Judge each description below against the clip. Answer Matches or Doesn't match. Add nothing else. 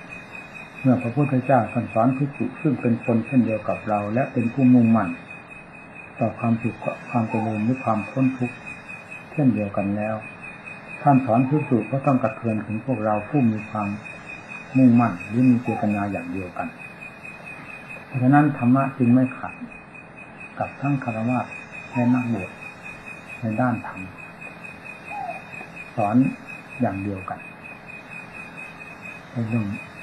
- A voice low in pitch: Matches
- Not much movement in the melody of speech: Doesn't match